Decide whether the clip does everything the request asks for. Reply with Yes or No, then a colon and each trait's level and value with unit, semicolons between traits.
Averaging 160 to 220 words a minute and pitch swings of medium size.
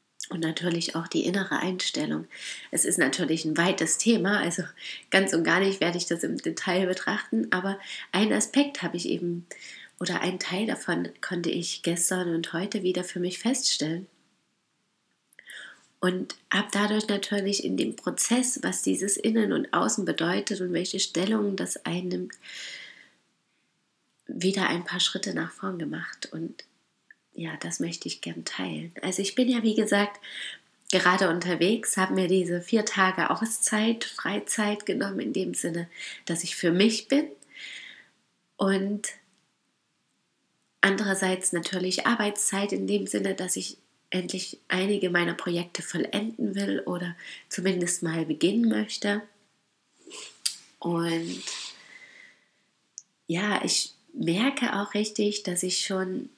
No: average, 135 wpm; average, 3.0 semitones